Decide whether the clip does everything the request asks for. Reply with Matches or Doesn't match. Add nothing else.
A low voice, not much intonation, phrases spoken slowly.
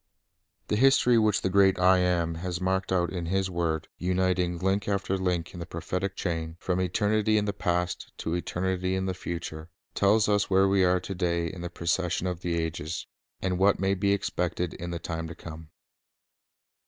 Doesn't match